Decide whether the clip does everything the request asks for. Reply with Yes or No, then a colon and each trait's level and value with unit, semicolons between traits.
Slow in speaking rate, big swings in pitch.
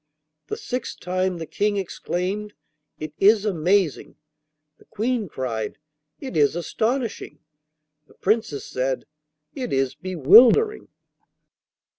Yes: slow, 105 wpm; wide, 6.4 semitones